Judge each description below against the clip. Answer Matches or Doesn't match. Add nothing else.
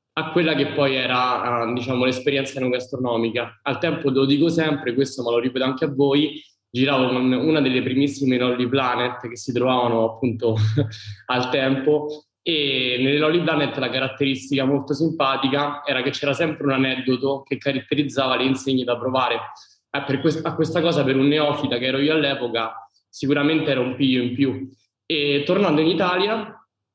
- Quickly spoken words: Matches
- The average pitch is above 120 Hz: Matches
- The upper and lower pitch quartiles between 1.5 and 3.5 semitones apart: Matches